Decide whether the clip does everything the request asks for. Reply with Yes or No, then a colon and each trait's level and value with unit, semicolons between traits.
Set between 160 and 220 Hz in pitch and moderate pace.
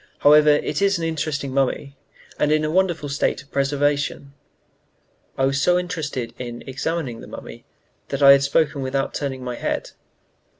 No: medium, 140 Hz; average, 165 wpm